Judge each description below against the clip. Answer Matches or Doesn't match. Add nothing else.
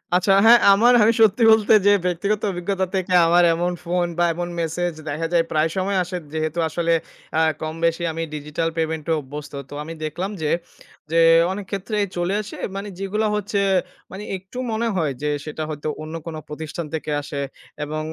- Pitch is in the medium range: Matches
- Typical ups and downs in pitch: Matches